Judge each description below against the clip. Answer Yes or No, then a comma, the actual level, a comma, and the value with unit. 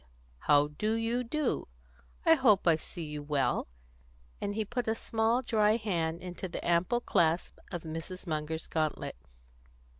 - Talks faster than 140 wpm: Yes, average, 150 wpm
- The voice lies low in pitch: No, medium, 185 Hz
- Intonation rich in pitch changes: Yes, wide, 5.9 semitones